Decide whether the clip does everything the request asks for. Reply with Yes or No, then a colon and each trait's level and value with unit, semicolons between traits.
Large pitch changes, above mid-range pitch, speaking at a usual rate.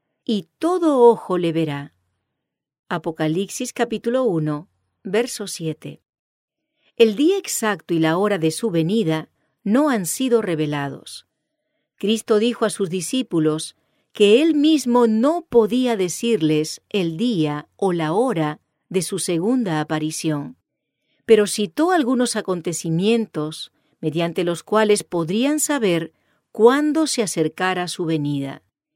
No: wide, 6.5 semitones; high, 195 Hz; slow, 120 wpm